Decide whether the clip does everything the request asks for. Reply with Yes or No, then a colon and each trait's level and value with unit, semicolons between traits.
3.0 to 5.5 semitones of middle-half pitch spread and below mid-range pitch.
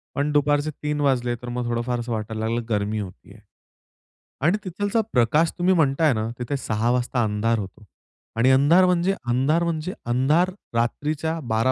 Yes: average, 5.2 semitones; low, 130 Hz